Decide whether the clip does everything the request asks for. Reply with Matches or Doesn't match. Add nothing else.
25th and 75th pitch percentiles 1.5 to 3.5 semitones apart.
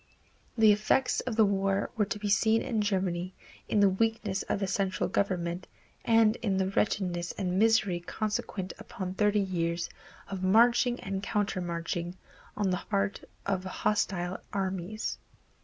Matches